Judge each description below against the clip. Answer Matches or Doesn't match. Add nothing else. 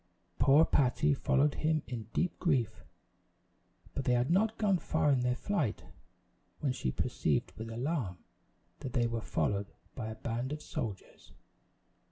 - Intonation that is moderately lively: Matches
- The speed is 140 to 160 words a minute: Matches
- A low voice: Matches